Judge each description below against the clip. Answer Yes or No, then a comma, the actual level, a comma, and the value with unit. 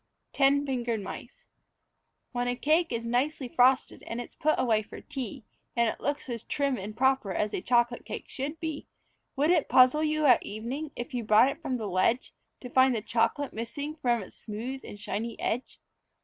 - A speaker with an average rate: Yes, average, 190 wpm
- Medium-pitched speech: No, high, 245 Hz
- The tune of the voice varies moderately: Yes, average, 3.6 semitones